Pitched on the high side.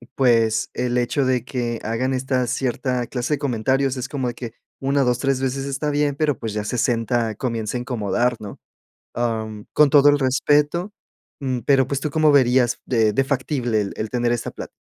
No: low, 125 Hz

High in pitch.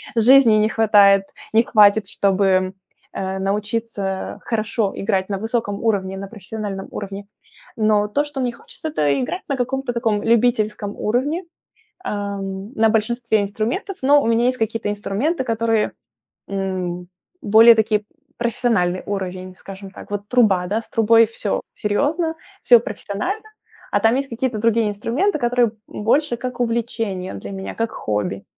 Yes: high, 215 Hz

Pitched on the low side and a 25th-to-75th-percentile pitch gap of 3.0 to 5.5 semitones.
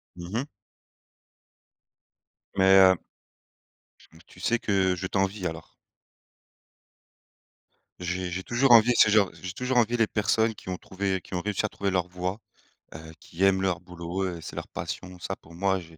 No: very low, 95 Hz; narrow, 2.5 semitones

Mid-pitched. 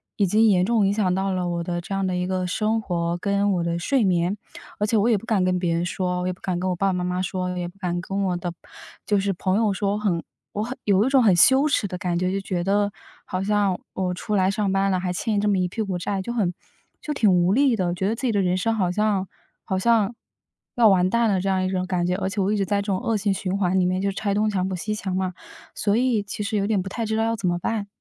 No: high, 195 Hz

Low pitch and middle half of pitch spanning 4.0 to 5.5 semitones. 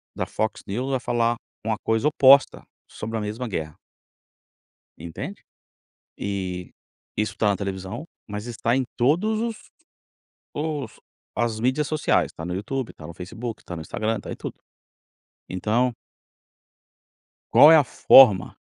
Yes: low, 115 Hz; average, 4.9 semitones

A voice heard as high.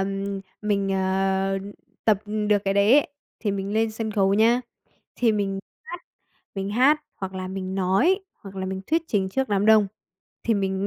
Yes: high, 200 Hz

